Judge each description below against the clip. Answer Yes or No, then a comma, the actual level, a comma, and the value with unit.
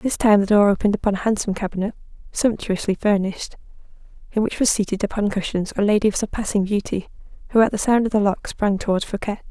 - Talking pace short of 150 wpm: No, average, 200 wpm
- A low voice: No, high, 205 Hz